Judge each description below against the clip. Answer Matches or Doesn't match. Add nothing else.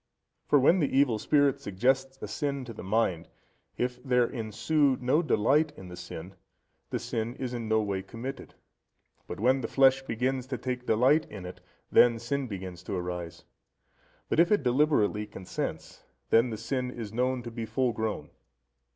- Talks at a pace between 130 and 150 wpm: Doesn't match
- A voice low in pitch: Matches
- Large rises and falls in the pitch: Doesn't match